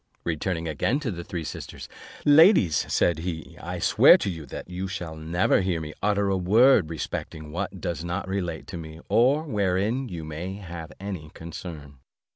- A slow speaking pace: No, average, 175 wpm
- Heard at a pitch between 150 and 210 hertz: No, very low, 90 Hz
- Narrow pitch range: No, average, 3.7 semitones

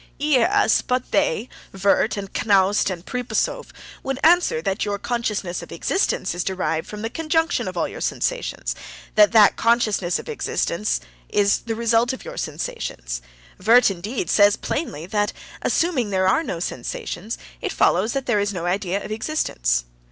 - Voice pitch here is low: No, high, 210 Hz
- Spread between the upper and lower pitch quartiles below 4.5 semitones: No, average, 4.8 semitones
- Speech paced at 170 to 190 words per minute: No, average, 155 wpm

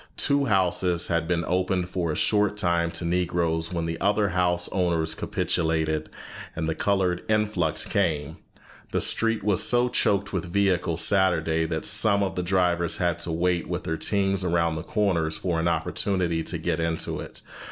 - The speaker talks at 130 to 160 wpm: No, average, 175 wpm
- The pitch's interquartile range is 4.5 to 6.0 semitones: No, average, 2.7 semitones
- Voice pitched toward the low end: Yes, very low, 90 Hz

